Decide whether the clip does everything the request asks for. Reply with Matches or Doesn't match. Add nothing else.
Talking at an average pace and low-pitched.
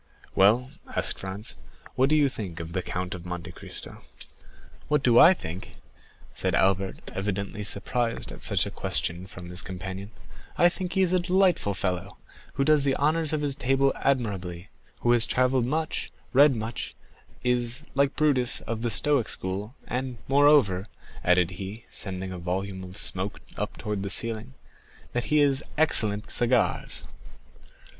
Matches